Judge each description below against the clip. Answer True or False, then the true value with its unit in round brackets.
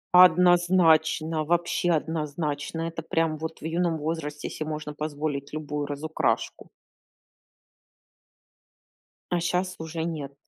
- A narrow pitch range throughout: True (1.9 semitones)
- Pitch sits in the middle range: True (160 Hz)